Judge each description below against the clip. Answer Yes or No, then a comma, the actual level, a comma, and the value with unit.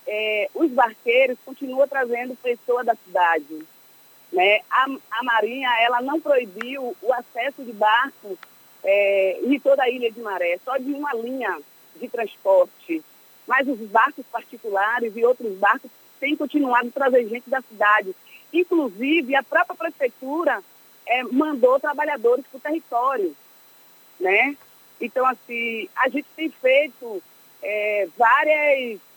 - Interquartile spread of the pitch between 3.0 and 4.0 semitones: Yes, average, 3.6 semitones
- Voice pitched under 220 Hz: No, very high, 255 Hz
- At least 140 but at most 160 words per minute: No, average, 130 wpm